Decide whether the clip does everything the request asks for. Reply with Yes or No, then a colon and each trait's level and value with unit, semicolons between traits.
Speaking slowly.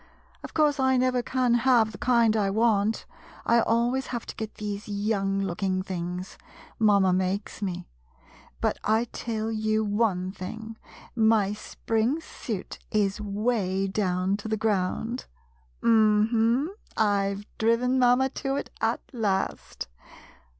No: average, 145 wpm